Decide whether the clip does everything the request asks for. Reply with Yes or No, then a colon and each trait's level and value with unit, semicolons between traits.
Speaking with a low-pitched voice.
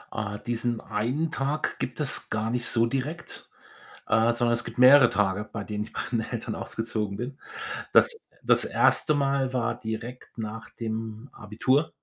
Yes: low, 120 Hz